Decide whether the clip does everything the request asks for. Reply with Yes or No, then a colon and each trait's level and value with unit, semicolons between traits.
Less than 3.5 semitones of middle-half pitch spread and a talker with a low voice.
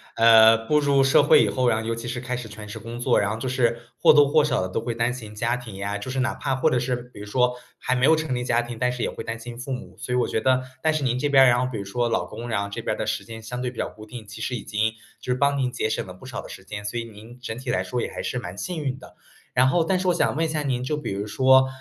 Yes: average, 2.8 semitones; low, 125 Hz